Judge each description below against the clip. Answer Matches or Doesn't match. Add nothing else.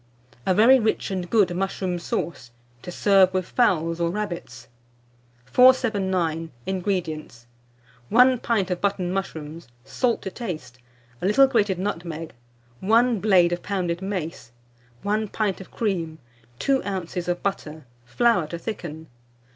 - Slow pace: Matches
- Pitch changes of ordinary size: Matches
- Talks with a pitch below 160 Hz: Doesn't match